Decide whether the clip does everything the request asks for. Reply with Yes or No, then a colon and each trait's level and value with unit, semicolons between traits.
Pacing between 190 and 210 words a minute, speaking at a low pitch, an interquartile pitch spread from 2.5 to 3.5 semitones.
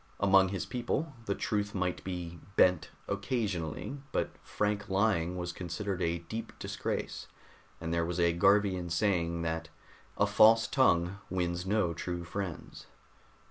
No: average, 140 wpm; very low, 90 Hz; average, 3.1 semitones